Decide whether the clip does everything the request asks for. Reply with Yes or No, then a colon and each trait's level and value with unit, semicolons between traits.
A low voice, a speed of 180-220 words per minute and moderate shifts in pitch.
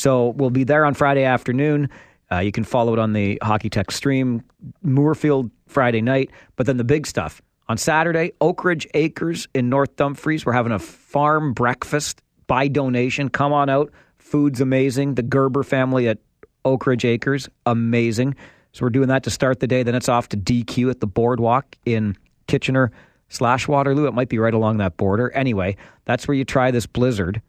Yes: low, 130 Hz; average, 190 wpm; average, 3.0 semitones